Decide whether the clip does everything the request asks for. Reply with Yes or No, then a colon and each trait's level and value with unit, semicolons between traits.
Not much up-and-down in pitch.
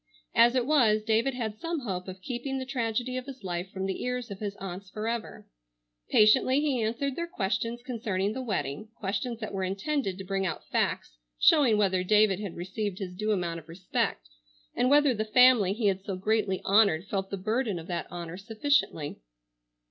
No: average, 4.6 semitones